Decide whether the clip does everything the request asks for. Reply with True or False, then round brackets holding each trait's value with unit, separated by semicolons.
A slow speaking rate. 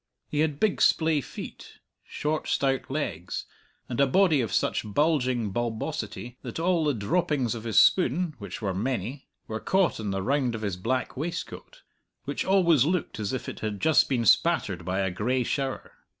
False (180 wpm)